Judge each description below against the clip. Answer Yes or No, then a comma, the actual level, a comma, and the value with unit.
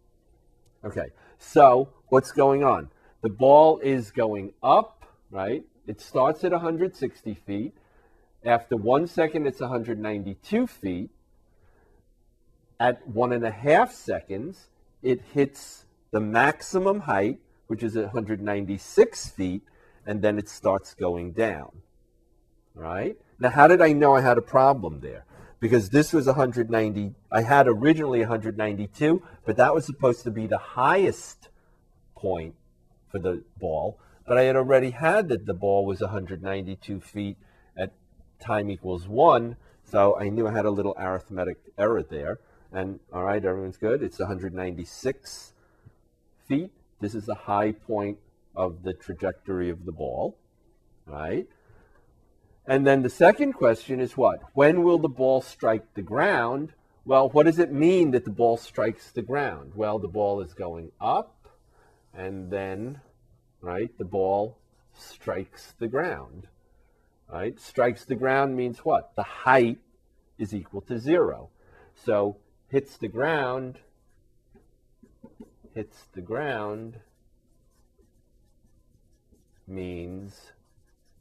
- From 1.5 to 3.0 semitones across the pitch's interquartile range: No, average, 4.9 semitones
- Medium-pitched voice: No, low, 110 Hz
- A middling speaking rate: No, slow, 130 wpm